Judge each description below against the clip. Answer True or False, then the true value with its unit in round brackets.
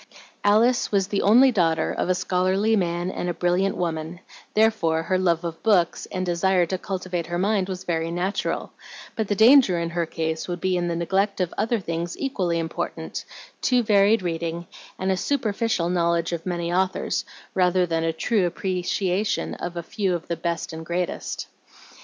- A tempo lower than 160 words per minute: False (180 wpm)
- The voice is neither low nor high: True (180 Hz)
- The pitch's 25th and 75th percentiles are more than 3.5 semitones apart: False (2.6 semitones)